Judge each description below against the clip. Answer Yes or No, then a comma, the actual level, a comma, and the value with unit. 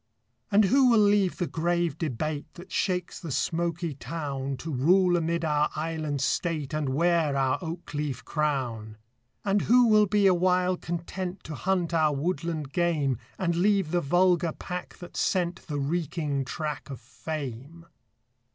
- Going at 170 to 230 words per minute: No, average, 150 wpm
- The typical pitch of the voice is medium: Yes, medium, 165 Hz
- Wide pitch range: No, average, 3.7 semitones